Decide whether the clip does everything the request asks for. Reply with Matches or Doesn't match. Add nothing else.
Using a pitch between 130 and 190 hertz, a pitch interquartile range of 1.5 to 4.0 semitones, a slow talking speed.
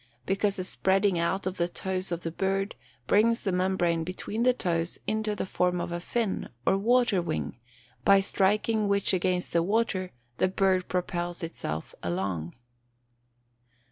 Doesn't match